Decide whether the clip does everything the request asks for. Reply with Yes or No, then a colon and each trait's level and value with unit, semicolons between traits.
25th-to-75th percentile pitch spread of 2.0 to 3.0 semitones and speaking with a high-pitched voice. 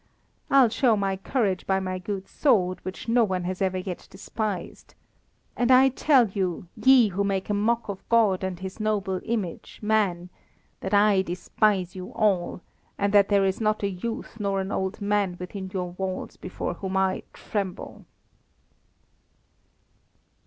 Yes: narrow, 2.4 semitones; high, 195 Hz